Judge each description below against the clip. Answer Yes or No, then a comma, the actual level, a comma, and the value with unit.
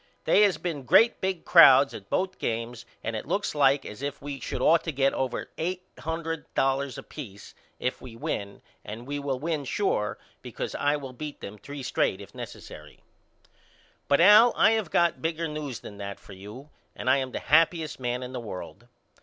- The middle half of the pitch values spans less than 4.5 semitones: No, average, 4.9 semitones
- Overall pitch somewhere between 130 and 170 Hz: Yes, medium, 140 Hz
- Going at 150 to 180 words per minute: No, average, 195 wpm